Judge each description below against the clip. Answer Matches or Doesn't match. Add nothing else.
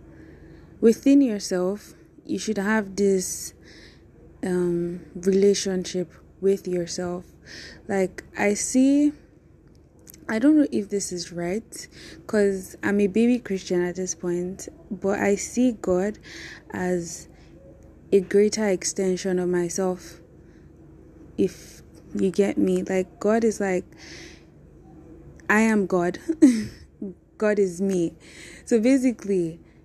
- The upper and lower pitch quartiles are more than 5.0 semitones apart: Doesn't match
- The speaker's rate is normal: Doesn't match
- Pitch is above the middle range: Matches